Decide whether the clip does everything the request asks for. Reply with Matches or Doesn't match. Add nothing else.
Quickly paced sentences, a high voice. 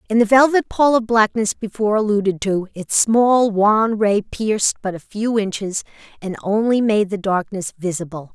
Doesn't match